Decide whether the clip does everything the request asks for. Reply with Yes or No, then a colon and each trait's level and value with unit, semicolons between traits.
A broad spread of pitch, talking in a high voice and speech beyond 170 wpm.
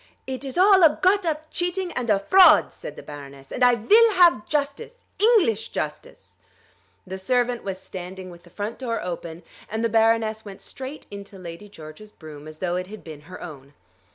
Yes: wide, 8.8 semitones; high, 220 Hz; average, 190 wpm